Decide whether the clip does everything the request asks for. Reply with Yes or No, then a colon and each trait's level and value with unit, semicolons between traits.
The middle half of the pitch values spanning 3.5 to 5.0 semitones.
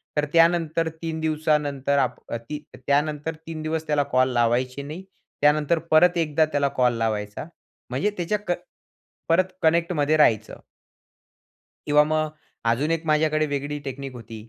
No: average, 2.7 semitones